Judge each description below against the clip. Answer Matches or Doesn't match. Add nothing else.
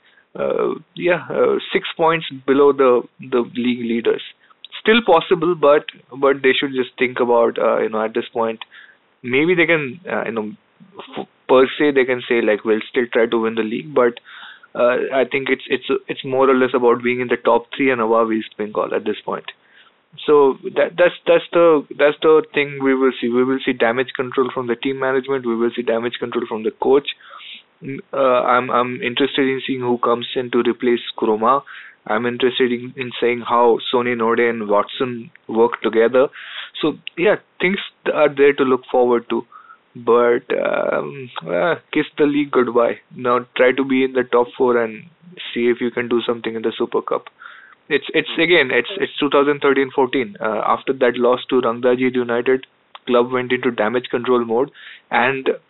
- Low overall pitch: Matches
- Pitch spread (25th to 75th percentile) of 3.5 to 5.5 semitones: Doesn't match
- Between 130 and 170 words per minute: Doesn't match